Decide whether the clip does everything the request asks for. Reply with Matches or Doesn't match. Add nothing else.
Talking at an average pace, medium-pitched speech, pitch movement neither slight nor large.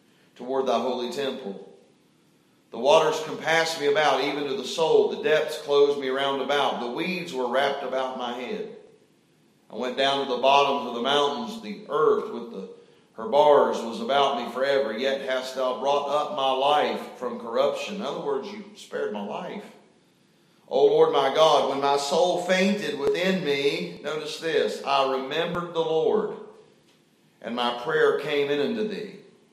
Doesn't match